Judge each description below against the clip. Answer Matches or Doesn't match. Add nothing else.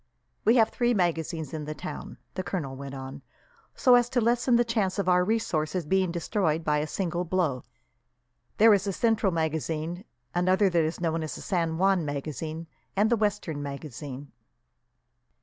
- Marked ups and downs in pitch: Doesn't match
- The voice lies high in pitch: Doesn't match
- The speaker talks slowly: Doesn't match